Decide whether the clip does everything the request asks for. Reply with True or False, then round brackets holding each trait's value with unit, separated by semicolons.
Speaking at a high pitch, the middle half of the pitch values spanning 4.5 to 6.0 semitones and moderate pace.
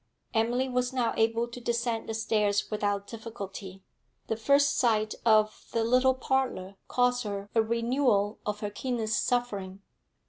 False (225 Hz; 3.0 semitones; 145 wpm)